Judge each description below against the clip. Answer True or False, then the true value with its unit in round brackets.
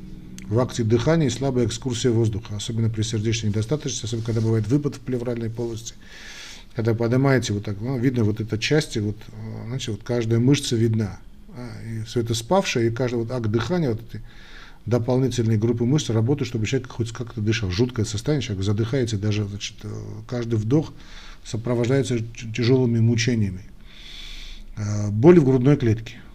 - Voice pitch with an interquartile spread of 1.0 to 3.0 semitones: True (2.7 semitones)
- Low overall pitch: True (115 Hz)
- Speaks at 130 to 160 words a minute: True (155 wpm)